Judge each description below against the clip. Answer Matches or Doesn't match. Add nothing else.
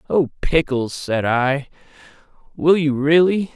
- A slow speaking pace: Matches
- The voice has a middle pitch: Matches